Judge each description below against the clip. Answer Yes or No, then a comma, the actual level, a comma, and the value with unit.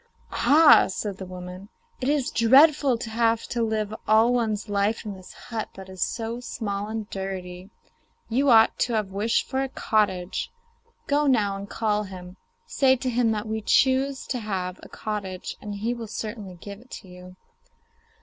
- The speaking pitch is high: Yes, high, 215 Hz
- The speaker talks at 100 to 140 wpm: No, average, 170 wpm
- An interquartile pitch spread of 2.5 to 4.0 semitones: Yes, average, 3.6 semitones